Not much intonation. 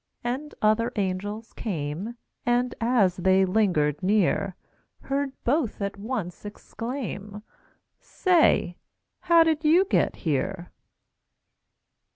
No: average, 5.1 semitones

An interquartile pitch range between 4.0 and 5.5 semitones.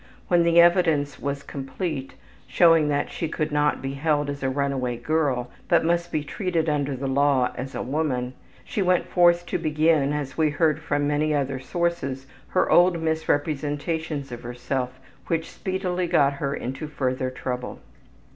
No: average, 3.2 semitones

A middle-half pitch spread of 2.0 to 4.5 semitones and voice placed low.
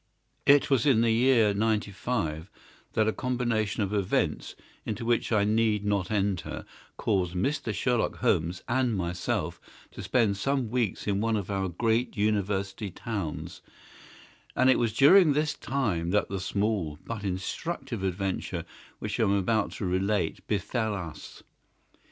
Yes: average, 3.5 semitones; low, 105 Hz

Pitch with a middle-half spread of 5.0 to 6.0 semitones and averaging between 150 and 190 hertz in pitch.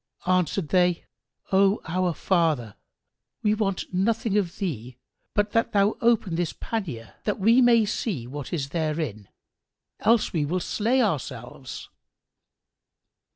Yes: wide, 5.5 semitones; medium, 185 Hz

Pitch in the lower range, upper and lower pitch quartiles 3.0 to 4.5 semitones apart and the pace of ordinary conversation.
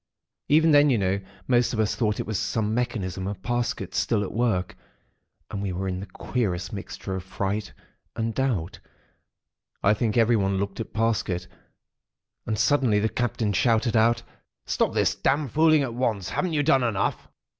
Yes: low, 110 Hz; average, 3.8 semitones; average, 170 wpm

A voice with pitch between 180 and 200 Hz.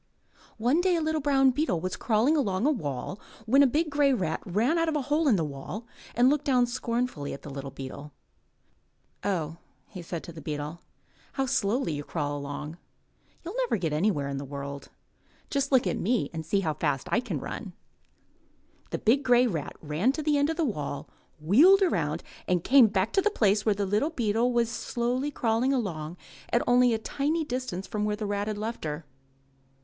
No: high, 220 Hz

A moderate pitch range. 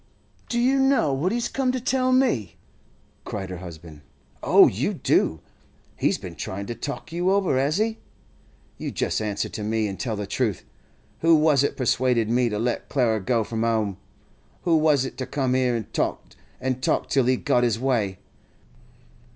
No: wide, 6.7 semitones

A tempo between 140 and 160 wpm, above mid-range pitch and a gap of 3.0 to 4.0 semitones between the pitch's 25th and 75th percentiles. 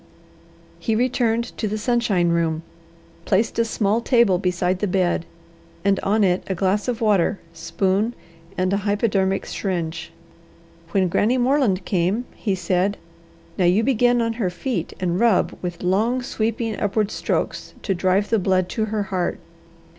Yes: average, 155 wpm; high, 200 Hz; average, 3.7 semitones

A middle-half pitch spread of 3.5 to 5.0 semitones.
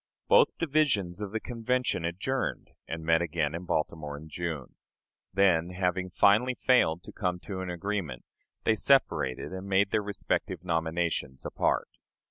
Yes: average, 4.2 semitones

